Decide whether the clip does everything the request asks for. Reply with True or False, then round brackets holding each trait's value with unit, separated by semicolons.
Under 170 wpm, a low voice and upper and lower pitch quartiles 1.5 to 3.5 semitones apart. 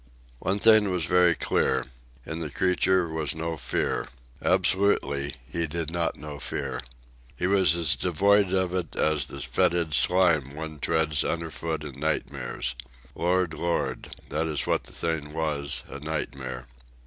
True (150 wpm; 80 Hz; 3.0 semitones)